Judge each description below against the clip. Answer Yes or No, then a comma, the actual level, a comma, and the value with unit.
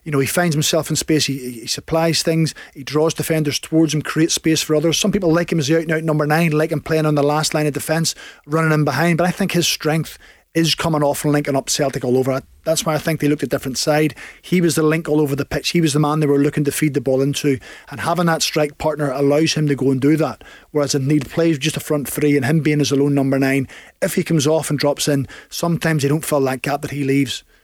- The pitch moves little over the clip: Yes, narrow, 2.1 semitones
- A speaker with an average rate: No, fast, 280 wpm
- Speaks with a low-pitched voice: No, medium, 150 Hz